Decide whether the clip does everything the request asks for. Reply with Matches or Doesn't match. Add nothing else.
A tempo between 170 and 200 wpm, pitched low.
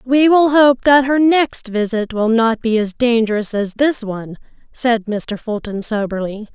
Doesn't match